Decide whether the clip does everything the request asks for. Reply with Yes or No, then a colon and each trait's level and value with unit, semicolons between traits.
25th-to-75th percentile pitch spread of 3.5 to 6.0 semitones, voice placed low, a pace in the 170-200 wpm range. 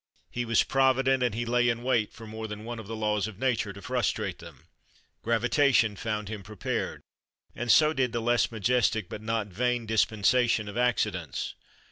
No: narrow, 2.5 semitones; low, 115 Hz; average, 180 wpm